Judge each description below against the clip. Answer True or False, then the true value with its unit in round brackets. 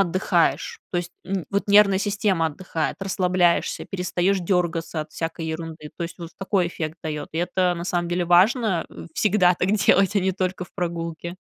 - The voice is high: False (180 Hz)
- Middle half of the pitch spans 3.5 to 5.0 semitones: False (2.4 semitones)